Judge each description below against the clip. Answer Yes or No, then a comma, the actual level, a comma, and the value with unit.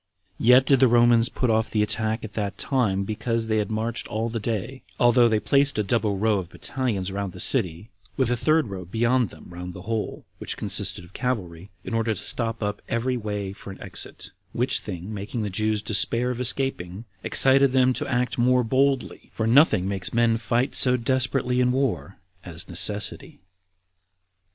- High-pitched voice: No, low, 115 Hz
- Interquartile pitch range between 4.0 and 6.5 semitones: No, average, 3.5 semitones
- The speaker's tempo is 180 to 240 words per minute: Yes, average, 190 wpm